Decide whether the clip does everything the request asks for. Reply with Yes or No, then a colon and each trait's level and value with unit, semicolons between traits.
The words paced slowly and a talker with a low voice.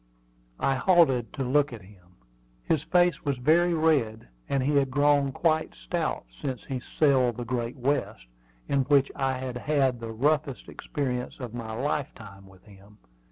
No: average, 160 wpm; low, 130 Hz